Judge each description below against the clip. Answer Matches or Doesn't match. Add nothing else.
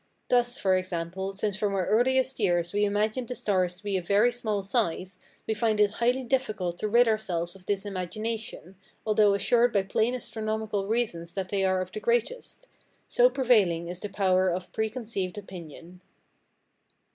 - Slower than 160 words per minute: Doesn't match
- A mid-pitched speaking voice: Doesn't match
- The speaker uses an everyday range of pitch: Matches